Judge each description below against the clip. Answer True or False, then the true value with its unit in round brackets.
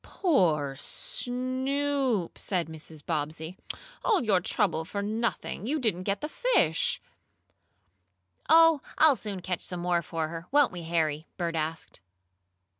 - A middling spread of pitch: False (7.9 semitones)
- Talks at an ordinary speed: False (130 wpm)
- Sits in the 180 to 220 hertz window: True (185 Hz)